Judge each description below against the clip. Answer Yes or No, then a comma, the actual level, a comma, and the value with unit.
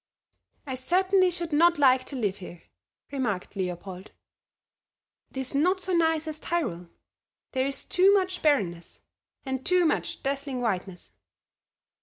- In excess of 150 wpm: No, slow, 135 wpm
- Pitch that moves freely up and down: Yes, wide, 8.7 semitones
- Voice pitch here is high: Yes, very high, 275 Hz